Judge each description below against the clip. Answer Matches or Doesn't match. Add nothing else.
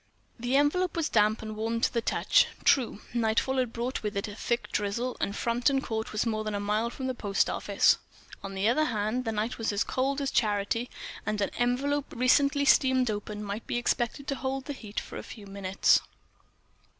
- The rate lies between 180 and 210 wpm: Matches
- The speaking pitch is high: Matches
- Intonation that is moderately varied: Matches